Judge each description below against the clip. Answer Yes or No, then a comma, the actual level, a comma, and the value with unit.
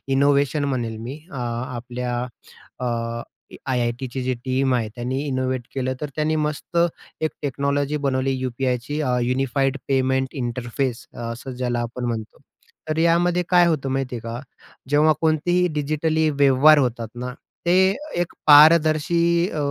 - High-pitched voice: No, low, 135 Hz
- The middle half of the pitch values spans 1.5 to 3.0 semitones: No, average, 3.6 semitones